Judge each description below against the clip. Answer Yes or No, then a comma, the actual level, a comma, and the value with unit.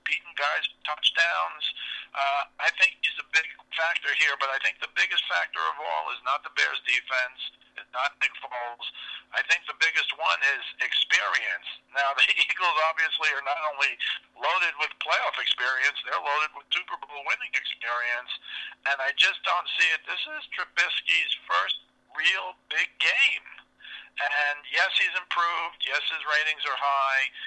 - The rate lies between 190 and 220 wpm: No, average, 165 wpm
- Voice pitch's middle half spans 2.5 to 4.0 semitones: Yes, average, 2.9 semitones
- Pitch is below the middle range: No, medium, 150 Hz